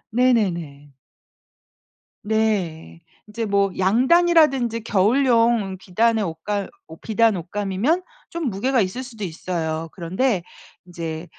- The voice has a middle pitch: No, high, 205 Hz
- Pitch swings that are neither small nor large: Yes, average, 5.0 semitones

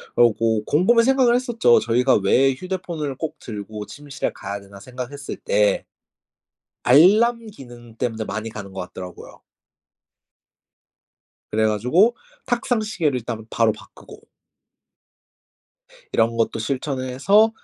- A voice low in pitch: Yes, low, 130 Hz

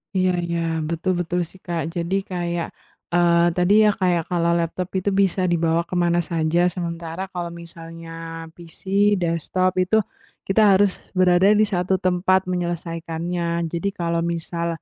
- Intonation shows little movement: Yes, narrow, 1.4 semitones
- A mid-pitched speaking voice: Yes, medium, 175 Hz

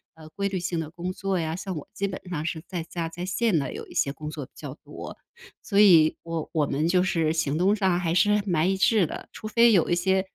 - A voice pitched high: No, medium, 175 Hz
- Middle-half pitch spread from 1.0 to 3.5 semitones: Yes, average, 3.2 semitones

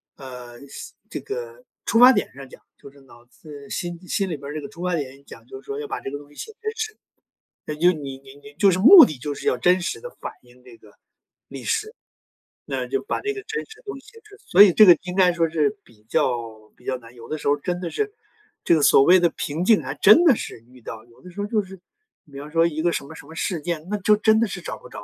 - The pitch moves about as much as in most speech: No, wide, 7.6 semitones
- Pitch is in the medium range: Yes, medium, 170 Hz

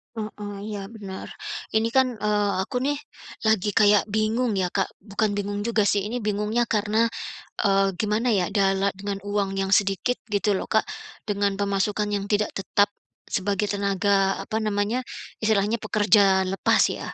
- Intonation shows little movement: Yes, narrow, 1.5 semitones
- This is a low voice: No, high, 205 Hz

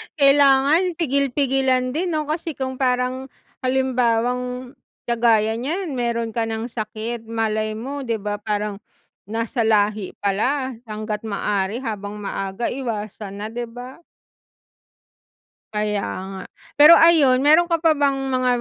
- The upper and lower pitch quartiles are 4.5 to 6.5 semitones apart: No, average, 4.0 semitones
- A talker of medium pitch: No, high, 245 Hz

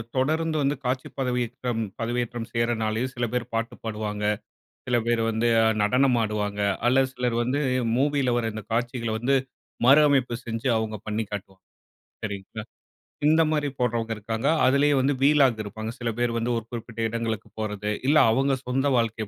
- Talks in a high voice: No, low, 120 Hz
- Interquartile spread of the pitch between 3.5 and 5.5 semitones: No, average, 2.8 semitones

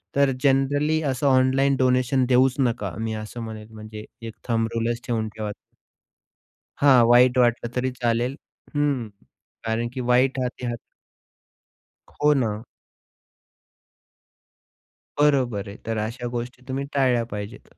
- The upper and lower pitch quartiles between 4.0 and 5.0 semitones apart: No, average, 2.8 semitones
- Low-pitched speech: Yes, low, 125 Hz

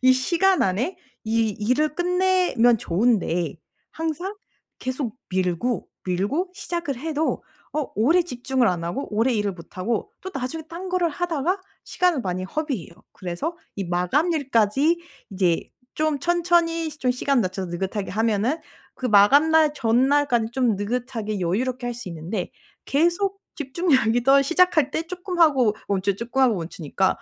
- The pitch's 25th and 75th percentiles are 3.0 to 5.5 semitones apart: No, wide, 7.9 semitones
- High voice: Yes, very high, 255 Hz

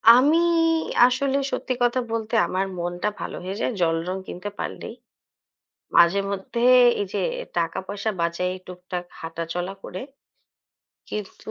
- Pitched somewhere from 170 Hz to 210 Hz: Yes, high, 190 Hz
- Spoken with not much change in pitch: No, wide, 5.5 semitones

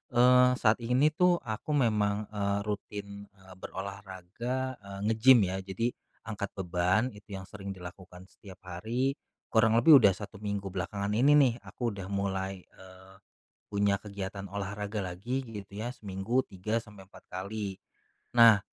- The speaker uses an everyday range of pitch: Yes, average, 3.1 semitones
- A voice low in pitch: Yes, low, 100 Hz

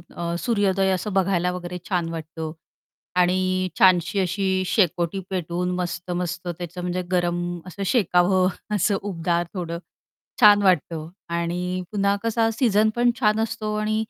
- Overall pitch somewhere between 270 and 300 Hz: No, medium, 185 Hz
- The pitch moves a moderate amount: No, narrow, 2.3 semitones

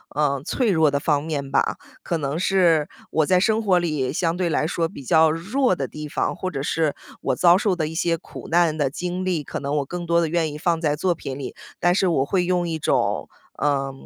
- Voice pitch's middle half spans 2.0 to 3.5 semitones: Yes, average, 3.2 semitones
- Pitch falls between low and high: Yes, medium, 165 Hz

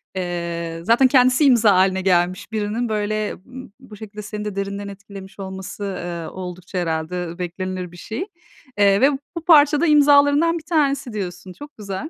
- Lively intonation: Yes, wide, 5.8 semitones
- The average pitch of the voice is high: Yes, high, 200 Hz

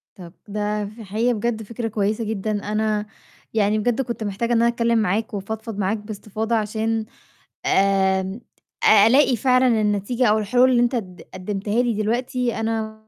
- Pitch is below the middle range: No, high, 220 Hz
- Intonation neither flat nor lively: No, narrow, 2.2 semitones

